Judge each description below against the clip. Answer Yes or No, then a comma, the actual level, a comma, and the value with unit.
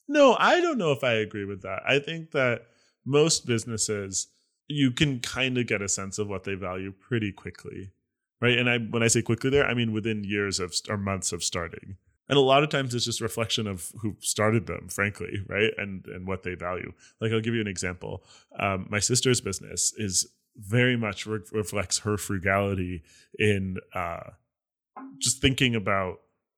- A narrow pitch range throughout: No, average, 4.0 semitones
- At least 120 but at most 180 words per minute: No, average, 190 wpm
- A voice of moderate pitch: No, low, 110 Hz